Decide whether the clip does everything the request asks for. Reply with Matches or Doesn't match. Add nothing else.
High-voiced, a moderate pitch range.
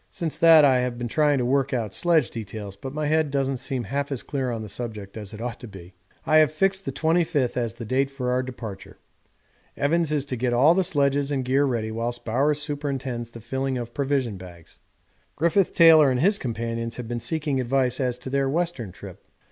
Doesn't match